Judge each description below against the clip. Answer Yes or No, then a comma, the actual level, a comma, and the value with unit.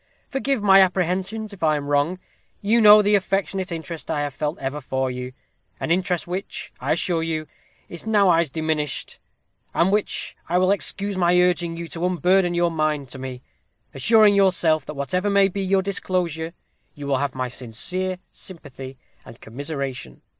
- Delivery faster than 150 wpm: Yes, average, 165 wpm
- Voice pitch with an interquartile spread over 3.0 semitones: Yes, average, 4.7 semitones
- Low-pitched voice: No, medium, 175 Hz